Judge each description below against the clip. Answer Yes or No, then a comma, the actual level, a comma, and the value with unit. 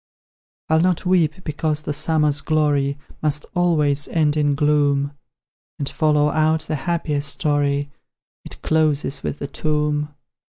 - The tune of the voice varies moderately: No, narrow, 1.5 semitones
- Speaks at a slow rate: Yes, slow, 130 wpm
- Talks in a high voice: No, medium, 150 Hz